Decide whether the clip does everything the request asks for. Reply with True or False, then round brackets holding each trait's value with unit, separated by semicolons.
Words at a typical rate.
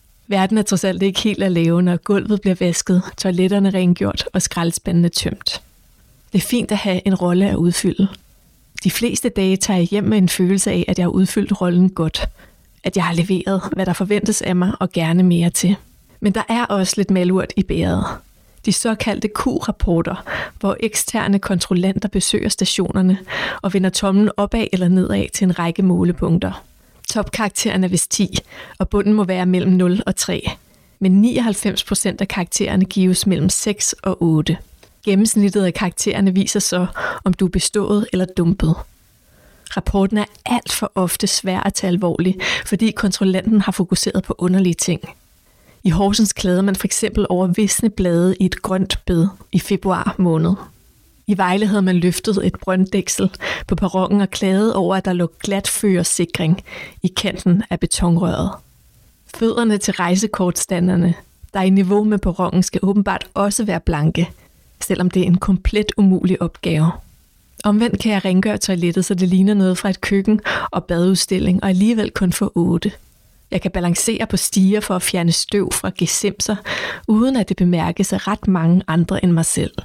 True (170 wpm)